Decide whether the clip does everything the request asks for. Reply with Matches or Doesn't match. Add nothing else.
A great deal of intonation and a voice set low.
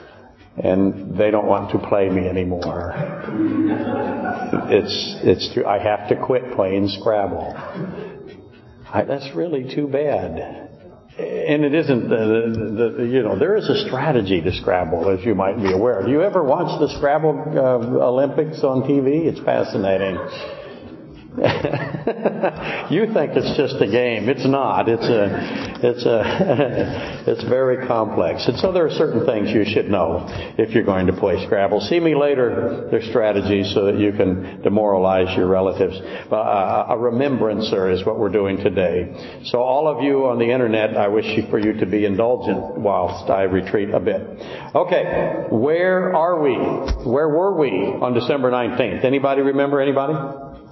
Matches